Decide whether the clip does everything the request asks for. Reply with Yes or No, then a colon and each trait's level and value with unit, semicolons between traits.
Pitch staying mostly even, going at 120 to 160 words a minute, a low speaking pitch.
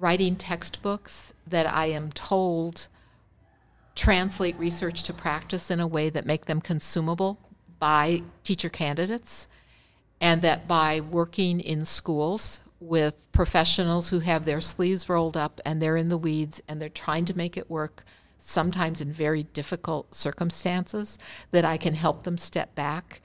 No: narrow, 2.3 semitones; average, 150 wpm; medium, 165 Hz